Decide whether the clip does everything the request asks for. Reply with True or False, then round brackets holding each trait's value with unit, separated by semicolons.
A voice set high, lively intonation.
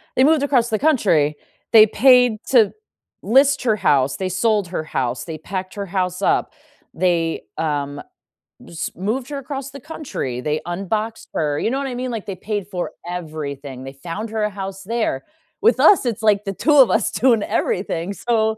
True (205 Hz; 6.3 semitones)